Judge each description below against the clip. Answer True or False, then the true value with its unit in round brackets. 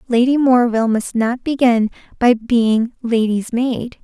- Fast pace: False (135 wpm)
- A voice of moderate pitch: False (240 Hz)